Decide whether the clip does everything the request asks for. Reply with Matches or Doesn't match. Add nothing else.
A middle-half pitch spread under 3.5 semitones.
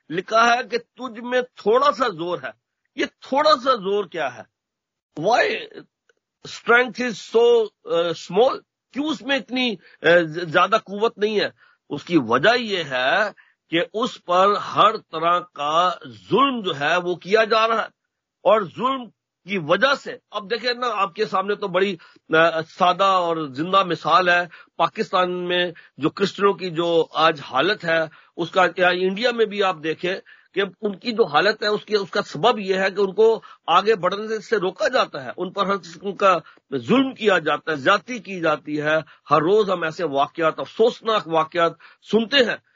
Doesn't match